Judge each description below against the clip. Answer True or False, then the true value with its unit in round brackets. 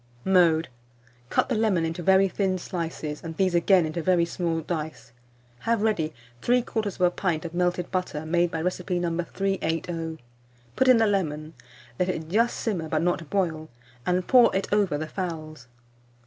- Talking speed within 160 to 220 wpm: True (165 wpm)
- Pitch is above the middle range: False (175 Hz)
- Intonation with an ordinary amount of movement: True (3.0 semitones)